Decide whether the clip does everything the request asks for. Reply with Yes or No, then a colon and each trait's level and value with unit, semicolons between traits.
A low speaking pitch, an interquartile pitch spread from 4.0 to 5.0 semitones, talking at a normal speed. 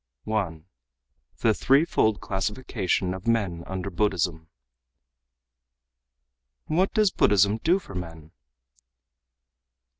No: low, 100 Hz; average, 4.5 semitones; slow, 85 wpm